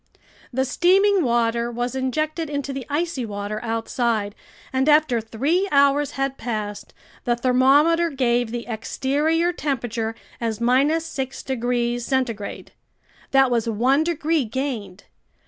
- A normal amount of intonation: Yes, average, 3.7 semitones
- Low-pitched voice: No, very high, 260 Hz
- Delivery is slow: Yes, slow, 120 wpm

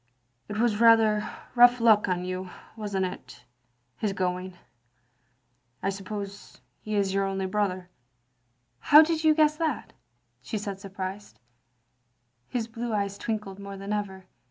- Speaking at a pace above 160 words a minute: No, average, 155 wpm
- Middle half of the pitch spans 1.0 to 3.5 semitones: Yes, average, 2.9 semitones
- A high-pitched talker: Yes, high, 200 Hz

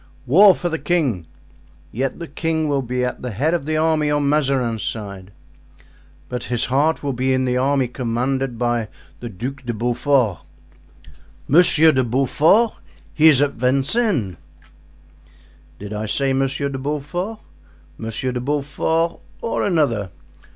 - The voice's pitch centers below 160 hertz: Yes, low, 135 Hz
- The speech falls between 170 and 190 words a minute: No, average, 145 wpm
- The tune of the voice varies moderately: Yes, average, 4.1 semitones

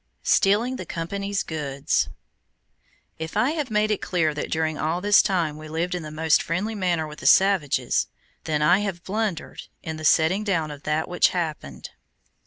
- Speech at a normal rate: Yes, average, 180 wpm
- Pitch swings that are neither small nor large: Yes, average, 4.2 semitones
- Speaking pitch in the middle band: Yes, medium, 170 Hz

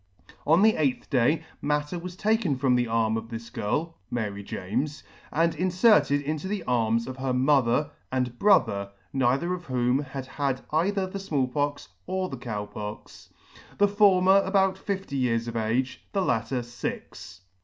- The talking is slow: No, average, 165 wpm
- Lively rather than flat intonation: Yes, wide, 7.1 semitones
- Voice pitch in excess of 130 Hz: Yes, medium, 140 Hz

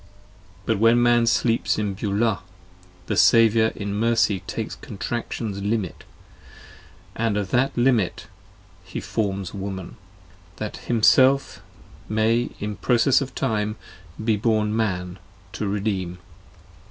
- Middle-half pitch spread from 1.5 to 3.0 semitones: Yes, narrow, 2.6 semitones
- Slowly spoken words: Yes, slow, 115 wpm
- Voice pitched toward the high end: No, low, 110 Hz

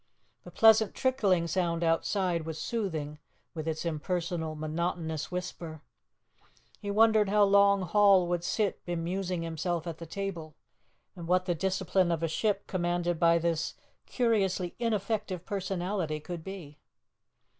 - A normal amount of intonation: Yes, average, 3.1 semitones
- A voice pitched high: No, medium, 175 Hz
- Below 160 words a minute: Yes, slow, 135 wpm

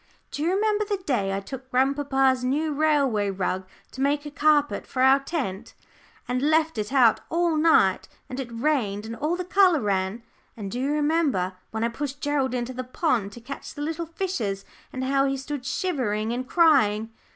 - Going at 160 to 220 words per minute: Yes, average, 190 wpm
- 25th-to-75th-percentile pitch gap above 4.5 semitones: Yes, average, 5.0 semitones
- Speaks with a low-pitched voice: No, very high, 270 Hz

